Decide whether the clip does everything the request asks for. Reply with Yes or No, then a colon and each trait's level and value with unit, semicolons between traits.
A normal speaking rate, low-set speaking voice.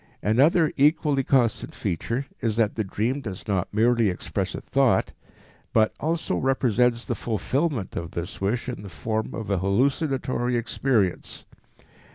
Yes: average, 145 wpm; low, 115 Hz